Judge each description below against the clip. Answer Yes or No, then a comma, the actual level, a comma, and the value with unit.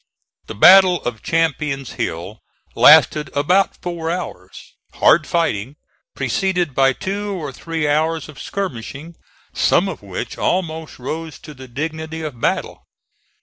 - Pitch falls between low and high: Yes, medium, 155 Hz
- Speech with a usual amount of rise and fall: Yes, average, 4.1 semitones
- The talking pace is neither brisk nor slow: No, slow, 130 wpm